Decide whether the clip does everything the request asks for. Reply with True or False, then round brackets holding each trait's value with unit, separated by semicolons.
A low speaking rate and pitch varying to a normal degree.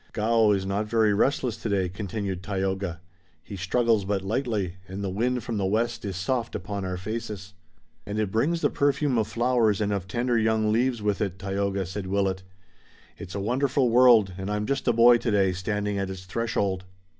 False (190 wpm; 3.3 semitones)